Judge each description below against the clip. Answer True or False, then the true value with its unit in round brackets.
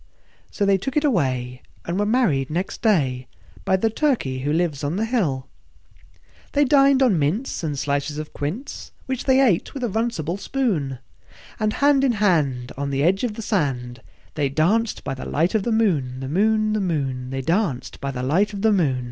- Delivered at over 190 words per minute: True (200 wpm)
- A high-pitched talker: False (175 Hz)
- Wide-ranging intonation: True (8.2 semitones)